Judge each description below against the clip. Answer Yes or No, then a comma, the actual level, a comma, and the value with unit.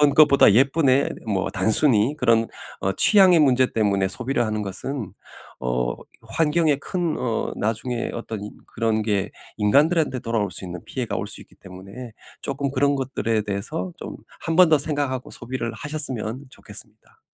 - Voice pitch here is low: Yes, low, 120 Hz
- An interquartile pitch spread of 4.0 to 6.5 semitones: Yes, average, 5.1 semitones